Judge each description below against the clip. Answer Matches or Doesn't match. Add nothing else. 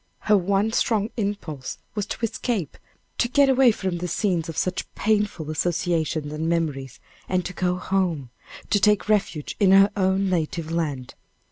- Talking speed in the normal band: Matches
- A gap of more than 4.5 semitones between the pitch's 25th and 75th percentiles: Doesn't match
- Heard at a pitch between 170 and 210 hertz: Matches